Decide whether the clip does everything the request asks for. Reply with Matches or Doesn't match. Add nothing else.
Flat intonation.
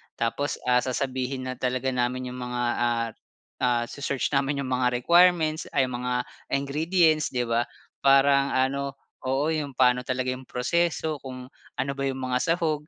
Matches